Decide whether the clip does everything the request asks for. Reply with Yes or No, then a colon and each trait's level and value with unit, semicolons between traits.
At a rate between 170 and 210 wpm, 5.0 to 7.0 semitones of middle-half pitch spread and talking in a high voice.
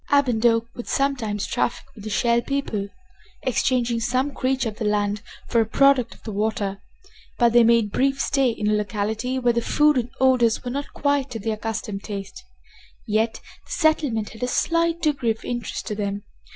No: average, 190 wpm; average, 3.5 semitones; high, 235 Hz